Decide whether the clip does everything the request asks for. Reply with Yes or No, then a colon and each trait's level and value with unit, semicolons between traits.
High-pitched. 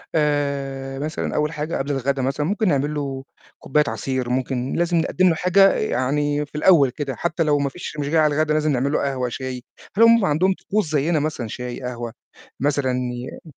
No: medium, 145 Hz